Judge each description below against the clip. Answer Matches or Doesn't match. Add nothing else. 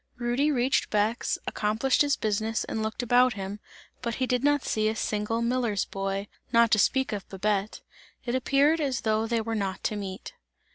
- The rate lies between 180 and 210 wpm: Matches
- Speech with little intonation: Doesn't match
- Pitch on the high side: Matches